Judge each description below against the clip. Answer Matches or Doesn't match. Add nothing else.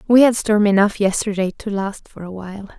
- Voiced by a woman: Matches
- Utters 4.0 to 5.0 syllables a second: Doesn't match